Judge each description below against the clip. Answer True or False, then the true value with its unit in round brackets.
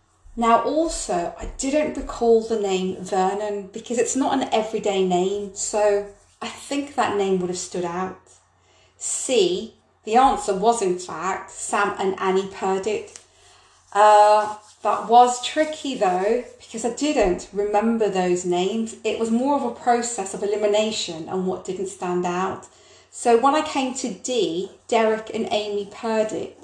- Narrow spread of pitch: False (4.6 semitones)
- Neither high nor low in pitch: False (215 Hz)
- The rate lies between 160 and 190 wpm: False (150 wpm)